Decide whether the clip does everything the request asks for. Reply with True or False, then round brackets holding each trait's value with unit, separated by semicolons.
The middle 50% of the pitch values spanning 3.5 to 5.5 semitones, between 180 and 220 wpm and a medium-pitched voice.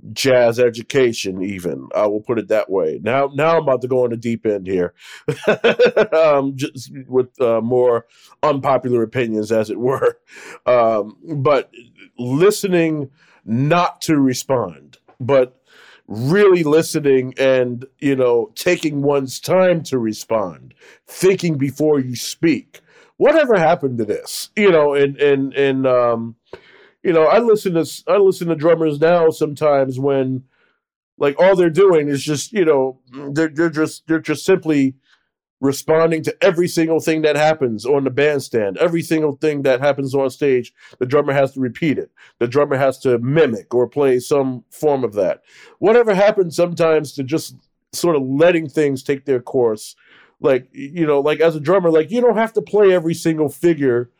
False (4.0 semitones; 165 wpm; 145 Hz)